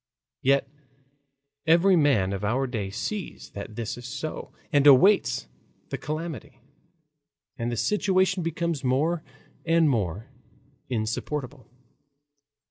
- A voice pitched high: No, medium, 140 Hz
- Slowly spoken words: Yes, slow, 110 wpm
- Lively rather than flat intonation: Yes, wide, 6.1 semitones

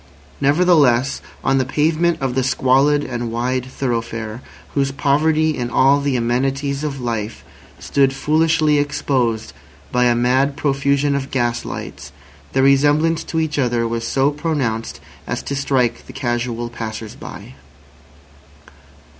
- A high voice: No, low, 135 Hz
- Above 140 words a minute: No, slow, 135 wpm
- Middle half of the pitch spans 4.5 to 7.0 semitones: No, average, 3.2 semitones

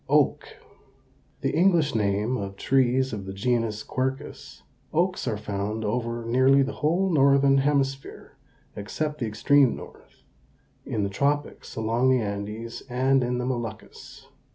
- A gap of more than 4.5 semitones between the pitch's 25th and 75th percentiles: No, average, 4.1 semitones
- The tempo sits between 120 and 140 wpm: Yes, slow, 135 wpm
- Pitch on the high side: No, low, 125 Hz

